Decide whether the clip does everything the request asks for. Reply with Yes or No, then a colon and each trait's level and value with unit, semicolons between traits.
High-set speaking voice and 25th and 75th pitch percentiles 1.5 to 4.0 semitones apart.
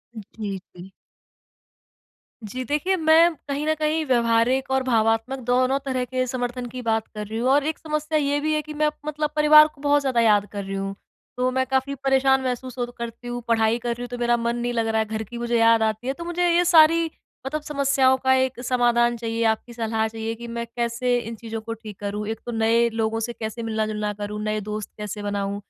Yes: high, 240 Hz; average, 3.3 semitones